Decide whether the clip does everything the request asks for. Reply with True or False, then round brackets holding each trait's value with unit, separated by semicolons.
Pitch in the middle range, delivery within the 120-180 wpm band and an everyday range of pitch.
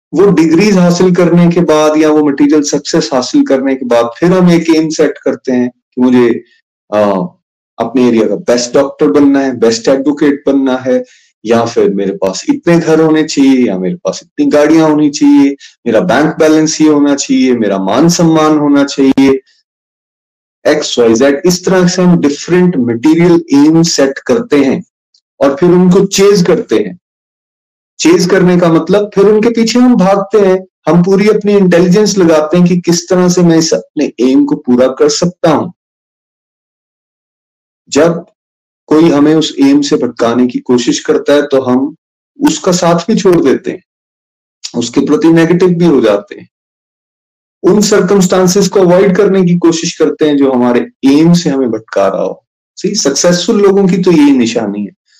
True (155 Hz; 175 wpm; 4.9 semitones)